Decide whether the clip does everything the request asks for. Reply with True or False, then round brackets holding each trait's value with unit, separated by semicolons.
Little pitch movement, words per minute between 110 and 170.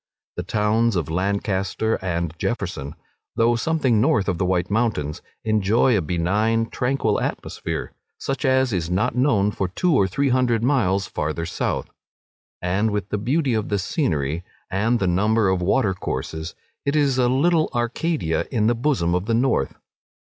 False (5.3 semitones; 165 wpm)